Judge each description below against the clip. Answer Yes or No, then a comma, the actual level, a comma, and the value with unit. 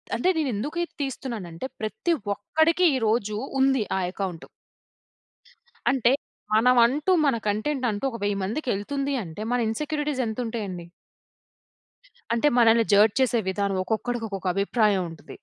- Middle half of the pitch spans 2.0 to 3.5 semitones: No, average, 4.7 semitones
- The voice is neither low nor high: No, high, 230 Hz